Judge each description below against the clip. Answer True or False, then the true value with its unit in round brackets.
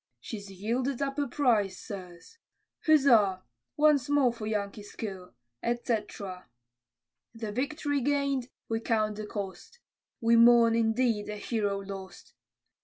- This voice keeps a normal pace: False (120 wpm)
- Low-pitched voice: False (225 Hz)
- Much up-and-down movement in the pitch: False (4.2 semitones)